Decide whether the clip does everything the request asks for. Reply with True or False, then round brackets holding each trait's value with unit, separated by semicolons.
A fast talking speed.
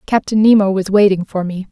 True (210 wpm)